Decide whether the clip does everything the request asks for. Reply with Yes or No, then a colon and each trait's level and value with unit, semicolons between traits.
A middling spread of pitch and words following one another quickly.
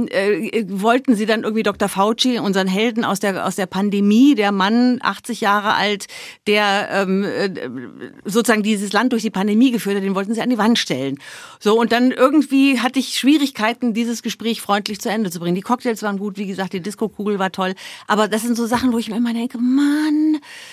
Yes: average, 3.3 semitones; fast, 205 wpm